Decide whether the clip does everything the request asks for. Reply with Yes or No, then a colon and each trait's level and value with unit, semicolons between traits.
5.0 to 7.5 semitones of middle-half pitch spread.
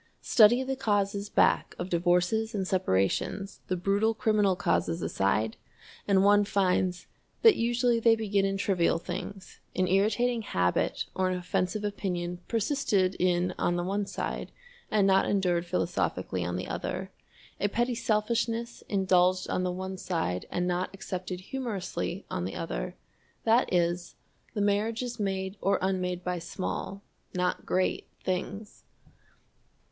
No: average, 2.8 semitones